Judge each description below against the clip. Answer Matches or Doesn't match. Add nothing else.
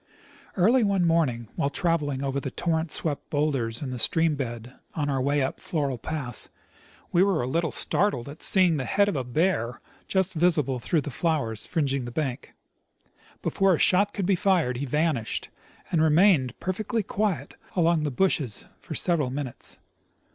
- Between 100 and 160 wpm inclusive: Doesn't match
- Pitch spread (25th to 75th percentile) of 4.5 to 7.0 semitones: Matches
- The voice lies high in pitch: Doesn't match